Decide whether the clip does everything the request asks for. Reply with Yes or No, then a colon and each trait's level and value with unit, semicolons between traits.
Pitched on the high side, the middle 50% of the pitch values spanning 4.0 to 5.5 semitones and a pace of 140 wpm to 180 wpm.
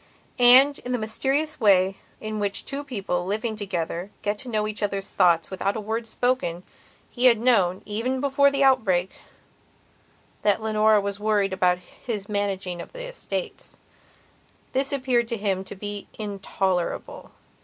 Yes: high, 215 Hz; average, 4.3 semitones; average, 155 wpm